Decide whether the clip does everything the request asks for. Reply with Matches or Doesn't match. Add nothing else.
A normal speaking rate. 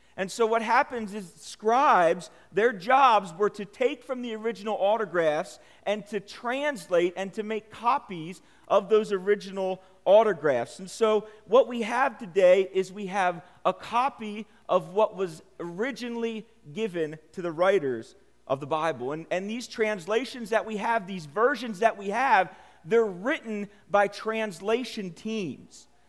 Matches